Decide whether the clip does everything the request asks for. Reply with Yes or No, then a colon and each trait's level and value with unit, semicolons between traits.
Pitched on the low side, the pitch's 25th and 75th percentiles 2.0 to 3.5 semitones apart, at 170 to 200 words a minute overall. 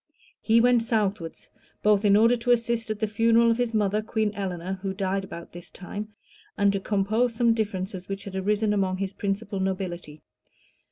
No: high, 205 Hz; average, 2.8 semitones; average, 180 wpm